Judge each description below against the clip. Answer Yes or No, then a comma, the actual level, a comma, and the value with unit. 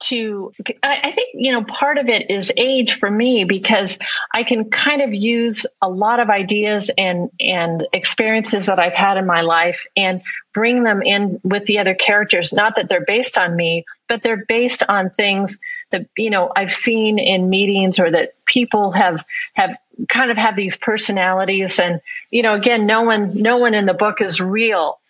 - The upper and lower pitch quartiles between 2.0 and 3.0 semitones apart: No, average, 3.5 semitones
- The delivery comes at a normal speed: Yes, average, 190 wpm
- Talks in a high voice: Yes, high, 210 Hz